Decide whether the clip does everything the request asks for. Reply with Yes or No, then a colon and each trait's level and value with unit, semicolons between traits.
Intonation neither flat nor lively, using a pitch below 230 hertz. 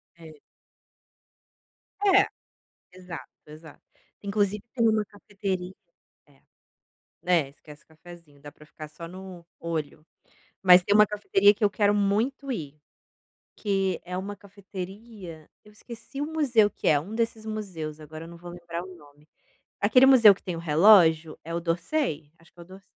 Yes: average, 4.3 semitones; medium, 185 Hz